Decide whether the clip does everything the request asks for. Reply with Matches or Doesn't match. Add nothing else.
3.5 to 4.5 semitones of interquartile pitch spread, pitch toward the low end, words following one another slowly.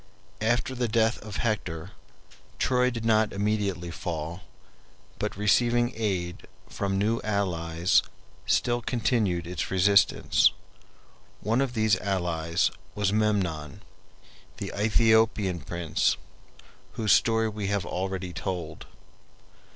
Matches